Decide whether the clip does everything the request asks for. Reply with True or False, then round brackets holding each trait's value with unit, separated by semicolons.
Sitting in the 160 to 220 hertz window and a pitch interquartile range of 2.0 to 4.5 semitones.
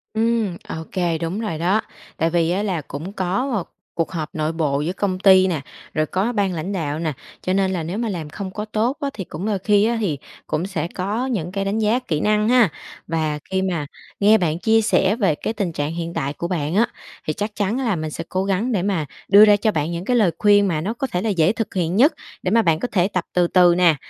True (190 Hz; 4.2 semitones)